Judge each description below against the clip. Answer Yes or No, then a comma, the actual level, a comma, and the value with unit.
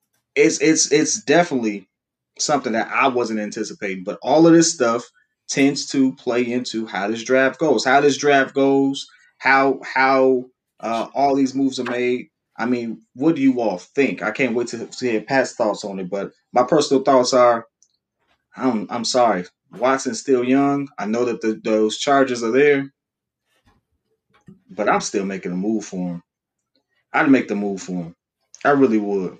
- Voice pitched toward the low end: Yes, low, 125 Hz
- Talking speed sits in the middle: Yes, average, 180 wpm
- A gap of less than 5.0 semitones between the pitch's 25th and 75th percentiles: Yes, average, 3.9 semitones